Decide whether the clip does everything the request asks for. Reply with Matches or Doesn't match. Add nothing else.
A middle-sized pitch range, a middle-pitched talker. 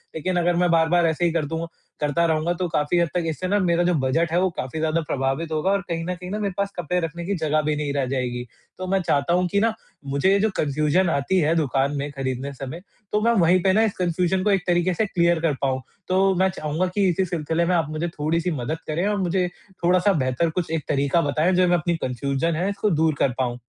Matches